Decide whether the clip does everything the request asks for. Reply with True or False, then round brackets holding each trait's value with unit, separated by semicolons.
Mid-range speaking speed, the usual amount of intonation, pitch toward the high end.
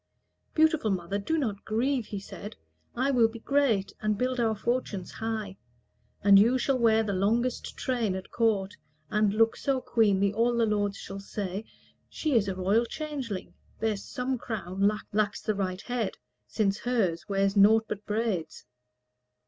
True (165 wpm; 3.2 semitones; 215 Hz)